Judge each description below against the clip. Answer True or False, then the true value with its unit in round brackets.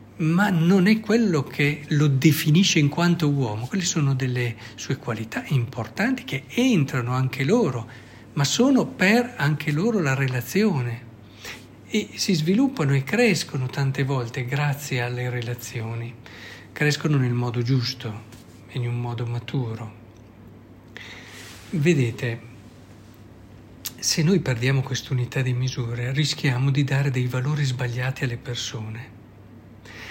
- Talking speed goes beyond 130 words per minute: False (120 wpm)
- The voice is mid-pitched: False (130 Hz)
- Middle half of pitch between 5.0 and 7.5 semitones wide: False (4.3 semitones)